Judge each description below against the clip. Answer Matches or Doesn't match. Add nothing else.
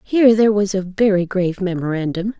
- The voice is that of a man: Doesn't match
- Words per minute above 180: Doesn't match